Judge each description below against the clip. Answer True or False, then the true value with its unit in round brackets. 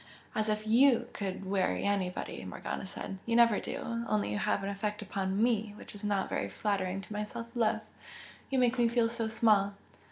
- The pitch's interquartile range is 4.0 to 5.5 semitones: False (2.6 semitones)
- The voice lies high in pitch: True (210 Hz)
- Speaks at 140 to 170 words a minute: False (195 wpm)